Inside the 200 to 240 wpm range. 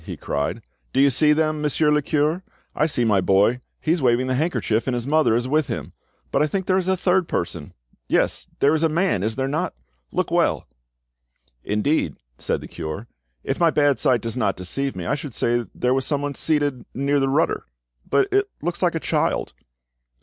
Yes: fast, 205 wpm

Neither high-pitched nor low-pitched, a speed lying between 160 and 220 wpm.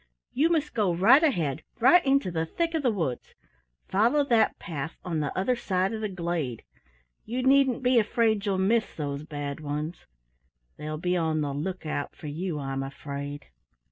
Yes: medium, 180 Hz; average, 170 wpm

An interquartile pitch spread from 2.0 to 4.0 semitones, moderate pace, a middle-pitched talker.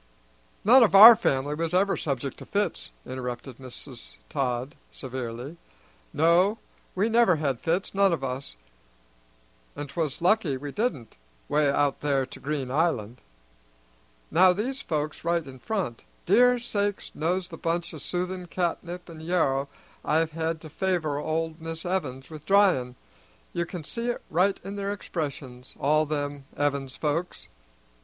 No: average, 5.0 semitones; average, 150 wpm; medium, 160 Hz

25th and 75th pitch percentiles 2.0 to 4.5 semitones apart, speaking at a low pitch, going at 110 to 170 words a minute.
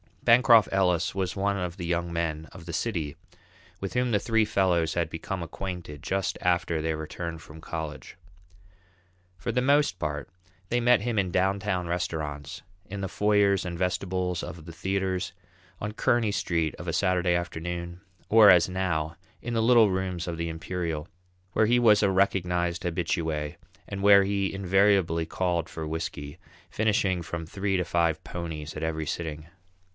Yes: average, 3.0 semitones; very low, 90 Hz; average, 165 wpm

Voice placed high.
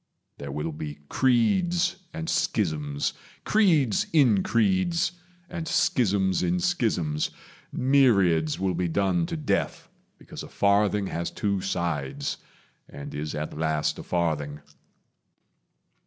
No: very low, 95 Hz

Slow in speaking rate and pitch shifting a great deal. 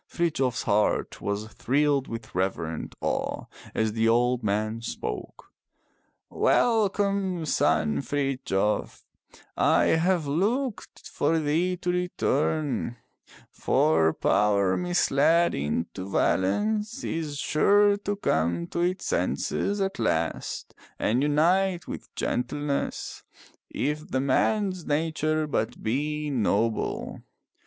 Yes: slow, 105 wpm; wide, 8.2 semitones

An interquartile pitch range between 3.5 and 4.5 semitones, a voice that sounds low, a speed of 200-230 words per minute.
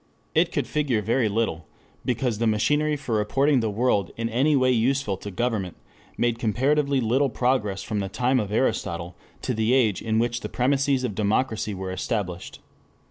No: average, 3.9 semitones; low, 115 Hz; average, 175 wpm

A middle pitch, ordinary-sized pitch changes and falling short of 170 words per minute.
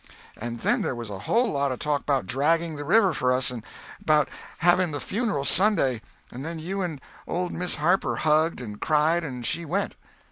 No: medium, 150 Hz; average, 4.8 semitones; average, 200 wpm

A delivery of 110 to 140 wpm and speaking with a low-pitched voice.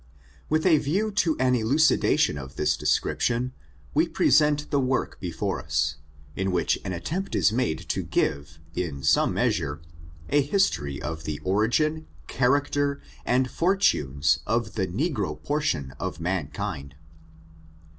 Yes: slow, 135 wpm; low, 115 Hz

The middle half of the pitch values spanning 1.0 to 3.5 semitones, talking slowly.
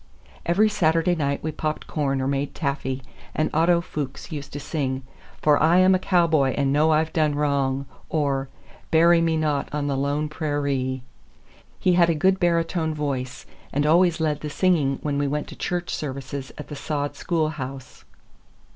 No: average, 2.9 semitones; average, 175 wpm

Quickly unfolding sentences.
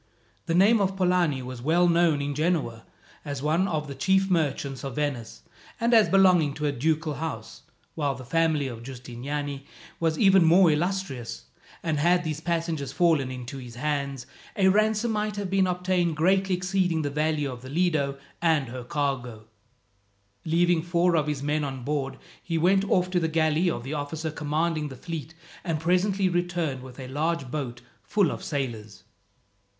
No: average, 175 wpm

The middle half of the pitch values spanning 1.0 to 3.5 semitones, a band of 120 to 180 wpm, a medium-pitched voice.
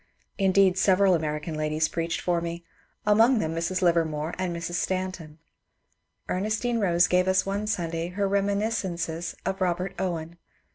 Yes: average, 2.8 semitones; average, 150 wpm; medium, 180 Hz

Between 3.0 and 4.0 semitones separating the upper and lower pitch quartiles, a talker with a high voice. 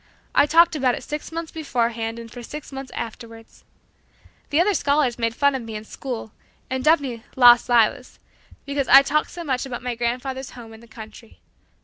Yes: average, 3.5 semitones; very high, 255 Hz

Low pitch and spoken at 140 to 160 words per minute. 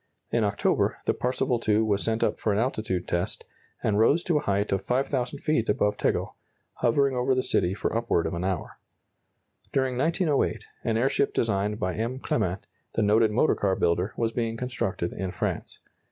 No: low, 115 Hz; average, 180 wpm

